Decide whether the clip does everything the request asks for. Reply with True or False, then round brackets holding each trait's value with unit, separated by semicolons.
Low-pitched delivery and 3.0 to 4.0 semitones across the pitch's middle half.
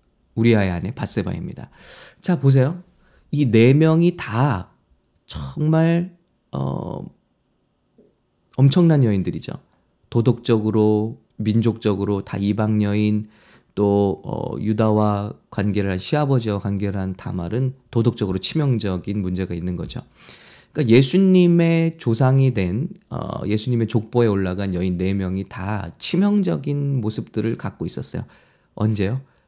False (110 Hz; 5.2 semitones)